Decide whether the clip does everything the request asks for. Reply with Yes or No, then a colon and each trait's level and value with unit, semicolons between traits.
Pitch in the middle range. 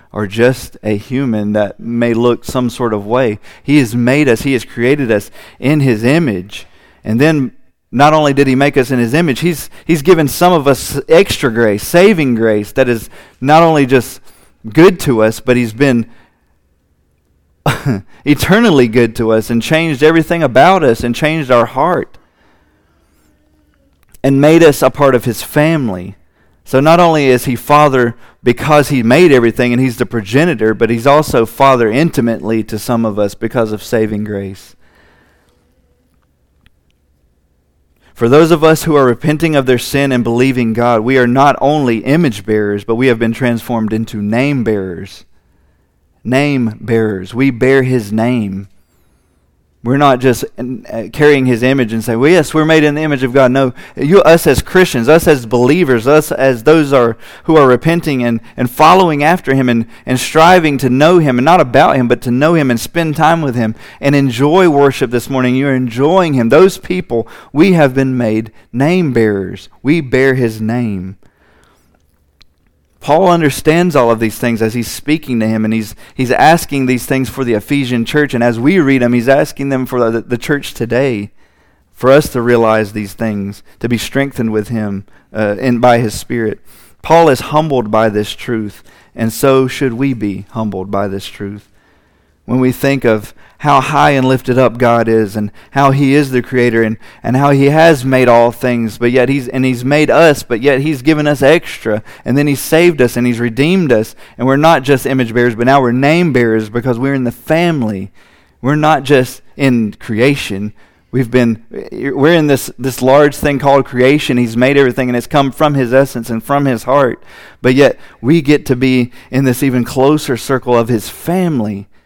No: low, 125 Hz